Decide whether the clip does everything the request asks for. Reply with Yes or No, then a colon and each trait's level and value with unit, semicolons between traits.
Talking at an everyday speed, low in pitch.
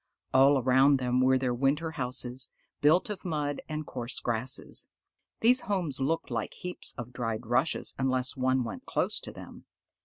Yes: average, 160 wpm; low, 130 Hz